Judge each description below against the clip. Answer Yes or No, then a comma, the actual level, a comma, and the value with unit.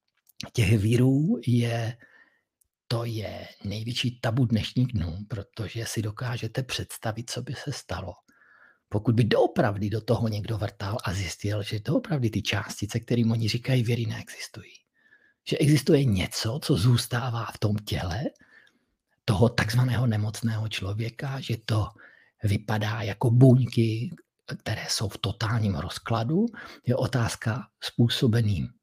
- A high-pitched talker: No, low, 115 Hz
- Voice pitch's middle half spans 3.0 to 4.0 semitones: No, narrow, 2.6 semitones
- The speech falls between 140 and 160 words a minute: No, average, 125 wpm